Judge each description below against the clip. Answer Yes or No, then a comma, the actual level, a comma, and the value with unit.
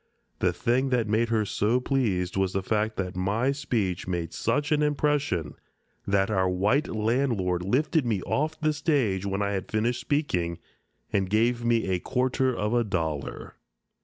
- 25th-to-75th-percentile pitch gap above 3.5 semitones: Yes, wide, 5.5 semitones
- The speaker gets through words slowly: No, average, 165 wpm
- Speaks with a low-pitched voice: Yes, low, 110 Hz